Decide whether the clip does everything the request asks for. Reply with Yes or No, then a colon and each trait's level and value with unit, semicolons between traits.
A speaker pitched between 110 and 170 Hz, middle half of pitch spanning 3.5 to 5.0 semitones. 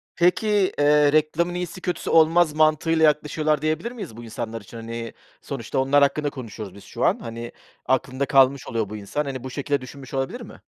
Yes: medium, 140 Hz; average, 4.7 semitones